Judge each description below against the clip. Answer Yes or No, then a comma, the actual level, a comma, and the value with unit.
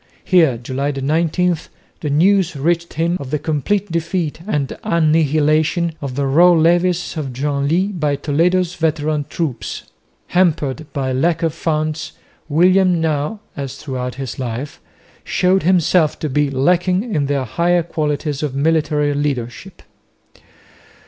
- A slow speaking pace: Yes, slow, 130 wpm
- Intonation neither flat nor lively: Yes, average, 3.4 semitones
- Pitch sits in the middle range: Yes, medium, 155 Hz